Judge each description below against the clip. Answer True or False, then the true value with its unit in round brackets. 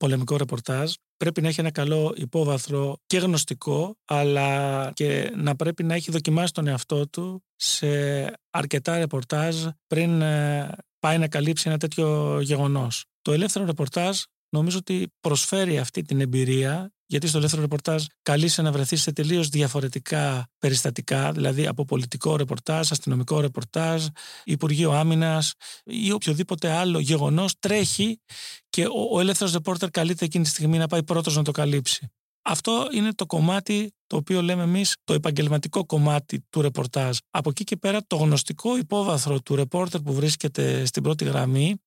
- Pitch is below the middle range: False (155 Hz)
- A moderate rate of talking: True (150 wpm)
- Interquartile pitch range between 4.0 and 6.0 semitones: False (3.1 semitones)